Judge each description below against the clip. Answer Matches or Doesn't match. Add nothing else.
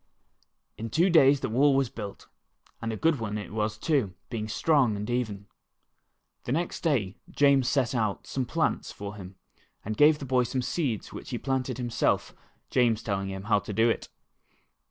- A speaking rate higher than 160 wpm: Matches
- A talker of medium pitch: Doesn't match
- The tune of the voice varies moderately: Matches